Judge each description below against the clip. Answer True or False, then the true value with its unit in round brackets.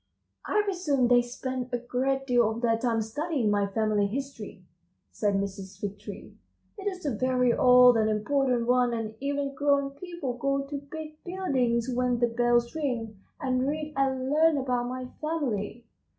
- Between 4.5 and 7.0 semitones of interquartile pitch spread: False (3.3 semitones)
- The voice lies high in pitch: True (250 Hz)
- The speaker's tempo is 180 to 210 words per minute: False (165 wpm)